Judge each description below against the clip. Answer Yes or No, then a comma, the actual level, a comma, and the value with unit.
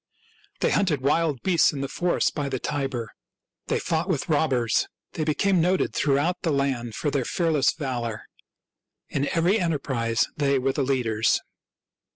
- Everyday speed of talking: Yes, average, 155 wpm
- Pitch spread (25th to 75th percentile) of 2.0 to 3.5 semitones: No, average, 4.0 semitones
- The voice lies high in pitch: No, medium, 140 Hz